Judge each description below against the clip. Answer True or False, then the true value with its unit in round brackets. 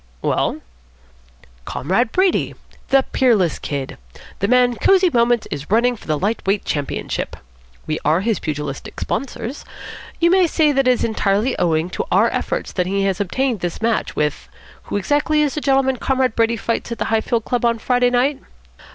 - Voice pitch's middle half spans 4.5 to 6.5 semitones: True (5.4 semitones)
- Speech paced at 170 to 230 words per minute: True (175 wpm)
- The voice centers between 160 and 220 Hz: False (235 Hz)